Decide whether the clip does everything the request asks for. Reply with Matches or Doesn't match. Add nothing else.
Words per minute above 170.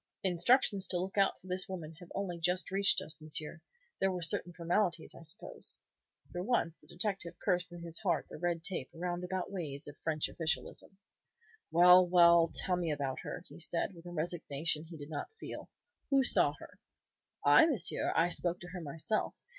Matches